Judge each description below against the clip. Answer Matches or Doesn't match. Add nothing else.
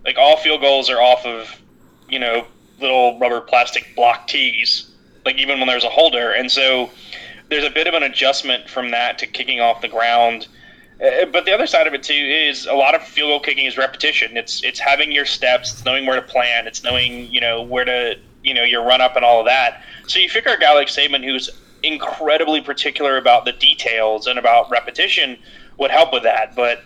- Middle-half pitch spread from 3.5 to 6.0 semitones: Doesn't match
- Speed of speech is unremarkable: Doesn't match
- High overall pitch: Doesn't match